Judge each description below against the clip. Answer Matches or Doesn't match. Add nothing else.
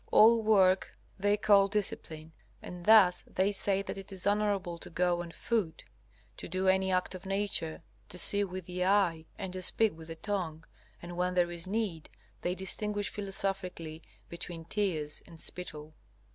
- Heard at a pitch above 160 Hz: Matches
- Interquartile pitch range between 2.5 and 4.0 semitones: Matches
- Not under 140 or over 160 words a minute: Doesn't match